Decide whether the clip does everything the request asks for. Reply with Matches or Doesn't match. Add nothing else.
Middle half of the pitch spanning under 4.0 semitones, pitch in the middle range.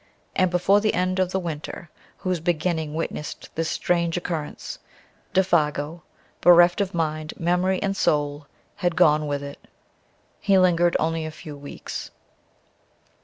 Matches